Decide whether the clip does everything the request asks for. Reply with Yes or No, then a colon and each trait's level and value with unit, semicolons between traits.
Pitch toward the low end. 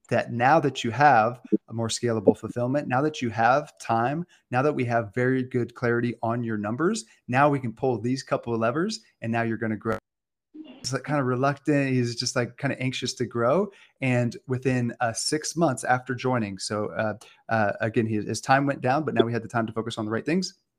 Yes: low, 125 Hz